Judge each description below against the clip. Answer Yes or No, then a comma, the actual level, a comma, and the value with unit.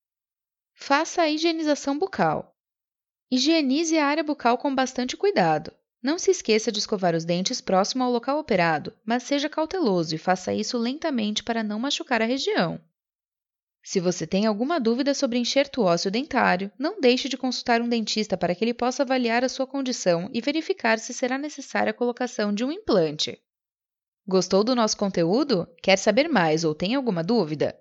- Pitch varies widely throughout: Yes, wide, 5.8 semitones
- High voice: Yes, high, 240 Hz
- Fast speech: No, average, 170 wpm